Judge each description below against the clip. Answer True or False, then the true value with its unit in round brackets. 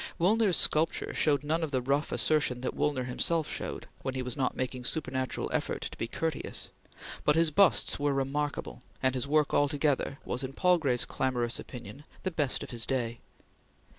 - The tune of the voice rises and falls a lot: False (3.3 semitones)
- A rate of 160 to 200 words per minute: True (175 wpm)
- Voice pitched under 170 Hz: True (140 Hz)